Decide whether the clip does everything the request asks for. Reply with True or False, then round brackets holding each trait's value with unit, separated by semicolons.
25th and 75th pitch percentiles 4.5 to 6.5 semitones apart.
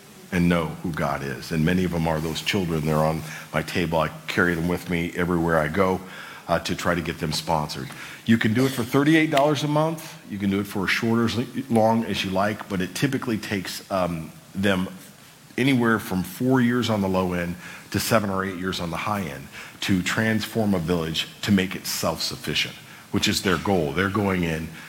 True (5.0 semitones)